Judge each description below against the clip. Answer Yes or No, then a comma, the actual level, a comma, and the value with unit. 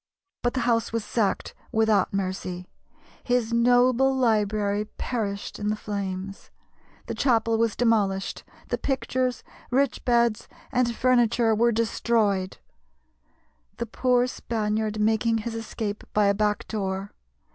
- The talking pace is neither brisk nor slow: No, slow, 125 wpm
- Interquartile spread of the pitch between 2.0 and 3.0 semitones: Yes, average, 2.7 semitones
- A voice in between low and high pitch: No, high, 225 Hz